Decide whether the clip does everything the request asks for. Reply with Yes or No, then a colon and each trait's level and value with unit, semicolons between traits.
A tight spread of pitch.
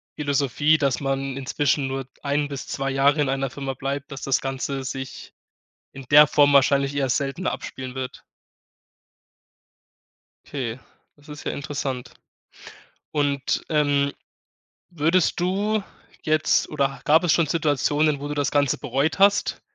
Yes: narrow, 1.7 semitones